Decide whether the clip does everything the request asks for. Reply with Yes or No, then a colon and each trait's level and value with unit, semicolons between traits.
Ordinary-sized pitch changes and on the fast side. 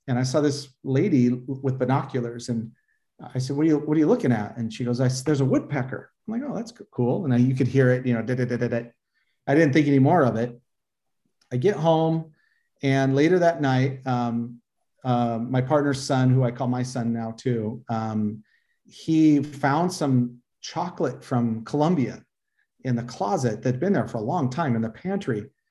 Yes: average, 3.3 semitones; fast, 210 wpm